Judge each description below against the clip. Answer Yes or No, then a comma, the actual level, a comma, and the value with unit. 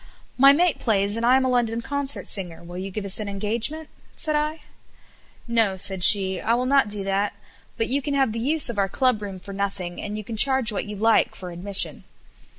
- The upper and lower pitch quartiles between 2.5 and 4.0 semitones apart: No, average, 4.8 semitones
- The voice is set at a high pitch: Yes, high, 215 Hz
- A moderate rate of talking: No, fast, 225 wpm